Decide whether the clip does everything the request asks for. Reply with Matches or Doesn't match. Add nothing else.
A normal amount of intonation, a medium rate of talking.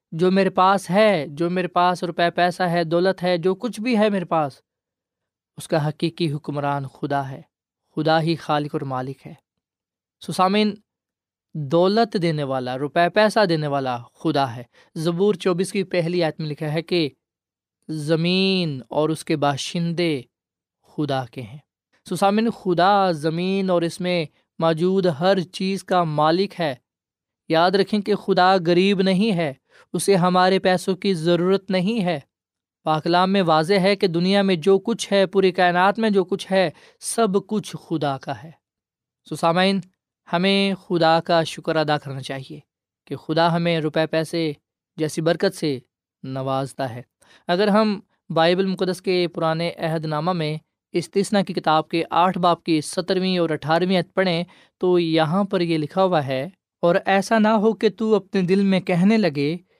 Matches